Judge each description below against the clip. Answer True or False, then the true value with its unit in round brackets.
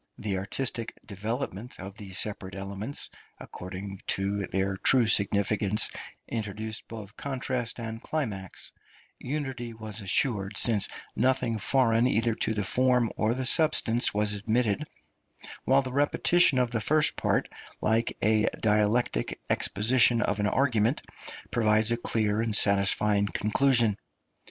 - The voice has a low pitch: True (110 Hz)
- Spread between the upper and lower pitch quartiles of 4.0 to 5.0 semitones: False (3.3 semitones)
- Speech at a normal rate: False (125 wpm)